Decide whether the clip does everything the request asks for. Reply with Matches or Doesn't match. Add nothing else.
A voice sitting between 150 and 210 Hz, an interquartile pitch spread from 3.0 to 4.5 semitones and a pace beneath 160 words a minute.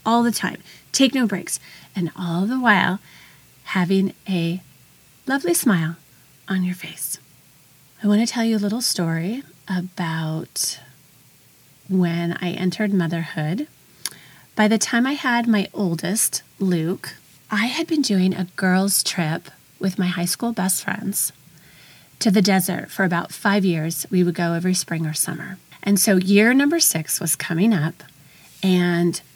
Matches